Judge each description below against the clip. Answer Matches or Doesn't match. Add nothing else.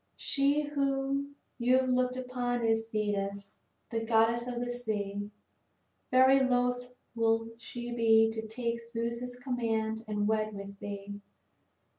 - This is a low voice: Doesn't match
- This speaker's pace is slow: Matches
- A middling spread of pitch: Doesn't match